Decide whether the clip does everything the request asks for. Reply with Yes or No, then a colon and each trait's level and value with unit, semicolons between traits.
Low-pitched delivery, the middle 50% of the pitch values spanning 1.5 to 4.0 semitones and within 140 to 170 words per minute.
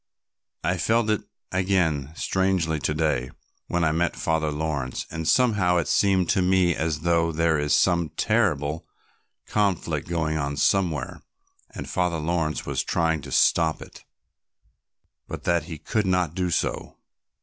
Yes: very low, 85 Hz; average, 2.9 semitones; average, 150 wpm